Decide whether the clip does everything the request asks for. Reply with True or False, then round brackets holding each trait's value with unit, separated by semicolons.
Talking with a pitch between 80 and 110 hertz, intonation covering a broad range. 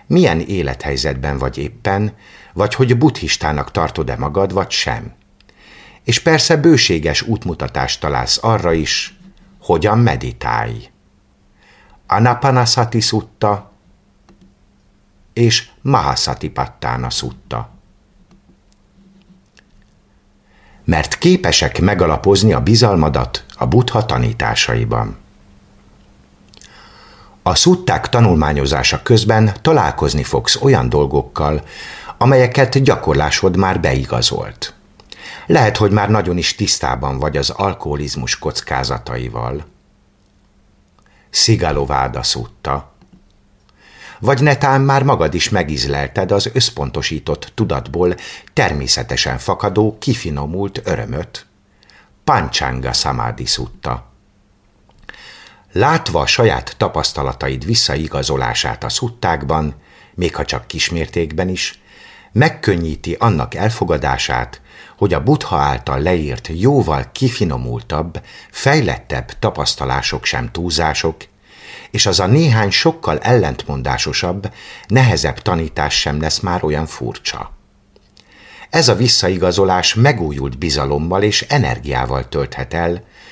True (95 Hz; 8.1 semitones)